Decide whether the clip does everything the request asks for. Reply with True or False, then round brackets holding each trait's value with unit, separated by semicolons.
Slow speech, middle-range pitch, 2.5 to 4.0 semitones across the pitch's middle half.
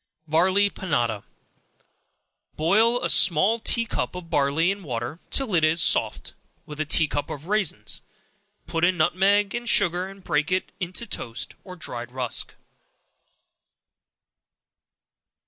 False (130 wpm; 175 Hz; 4.9 semitones)